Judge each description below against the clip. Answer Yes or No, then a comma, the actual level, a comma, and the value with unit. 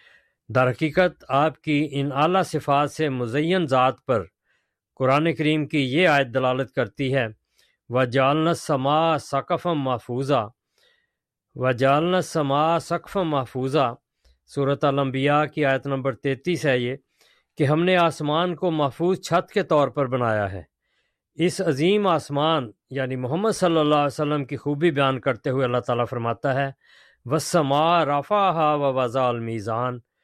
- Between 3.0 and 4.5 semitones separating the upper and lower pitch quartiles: Yes, average, 3.5 semitones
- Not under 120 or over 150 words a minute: Yes, average, 140 wpm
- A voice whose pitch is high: No, medium, 145 Hz